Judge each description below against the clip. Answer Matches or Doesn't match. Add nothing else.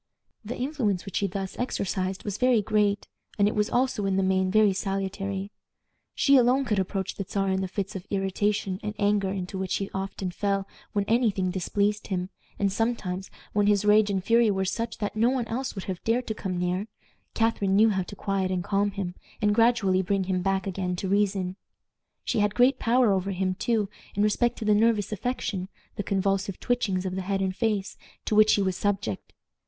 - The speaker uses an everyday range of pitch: Doesn't match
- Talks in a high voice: Matches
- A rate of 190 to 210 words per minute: Matches